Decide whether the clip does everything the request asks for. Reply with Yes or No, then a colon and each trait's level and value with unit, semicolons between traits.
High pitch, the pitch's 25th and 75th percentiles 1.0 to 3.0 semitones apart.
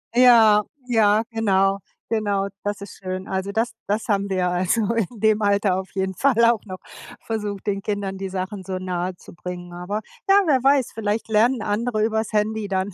Yes: high, 205 Hz; narrow, 2.6 semitones